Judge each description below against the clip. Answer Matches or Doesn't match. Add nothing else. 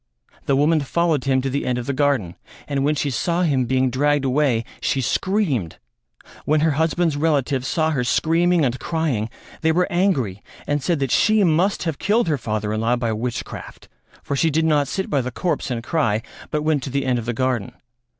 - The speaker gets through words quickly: Matches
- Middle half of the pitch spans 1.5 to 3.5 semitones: Doesn't match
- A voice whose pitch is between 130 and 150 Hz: Matches